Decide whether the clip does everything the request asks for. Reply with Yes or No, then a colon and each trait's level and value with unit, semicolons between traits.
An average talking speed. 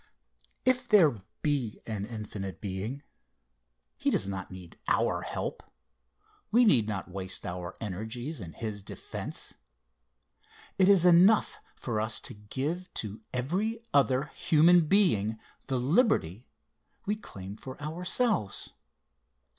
No: slow, 120 wpm